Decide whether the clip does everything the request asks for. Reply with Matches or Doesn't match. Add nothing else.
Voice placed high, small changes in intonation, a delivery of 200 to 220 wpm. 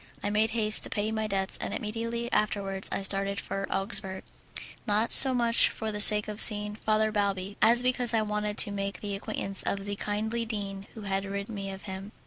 Matches